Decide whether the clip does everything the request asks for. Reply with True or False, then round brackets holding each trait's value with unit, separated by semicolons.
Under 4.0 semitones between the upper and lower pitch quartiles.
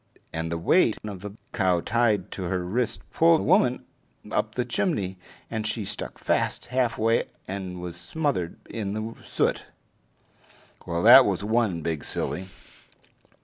False (4.7 semitones)